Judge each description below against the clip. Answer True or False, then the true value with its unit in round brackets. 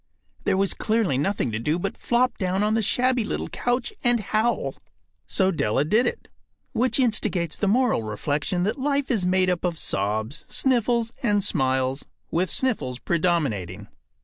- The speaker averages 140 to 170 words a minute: True (160 wpm)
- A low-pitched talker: False (190 Hz)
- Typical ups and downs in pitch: False (8.1 semitones)